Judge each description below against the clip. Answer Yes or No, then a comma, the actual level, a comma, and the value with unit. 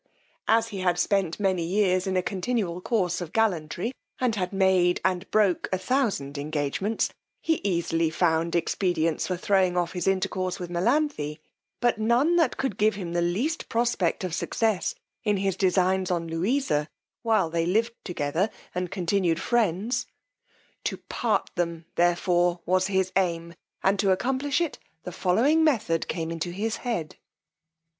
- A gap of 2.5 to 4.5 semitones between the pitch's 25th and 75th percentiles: Yes, average, 4.1 semitones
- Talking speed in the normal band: Yes, average, 155 wpm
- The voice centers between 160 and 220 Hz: Yes, medium, 185 Hz